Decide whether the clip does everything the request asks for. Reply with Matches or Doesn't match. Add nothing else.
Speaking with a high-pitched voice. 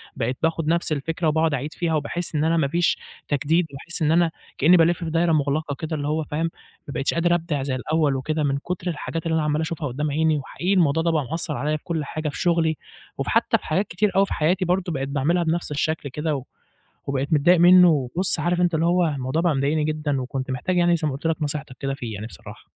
Doesn't match